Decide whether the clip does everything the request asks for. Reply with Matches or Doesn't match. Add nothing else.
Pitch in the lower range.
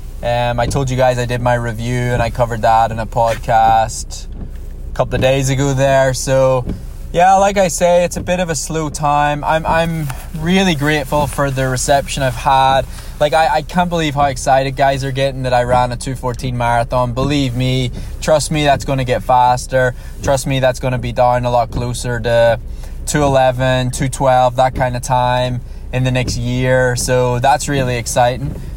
Matches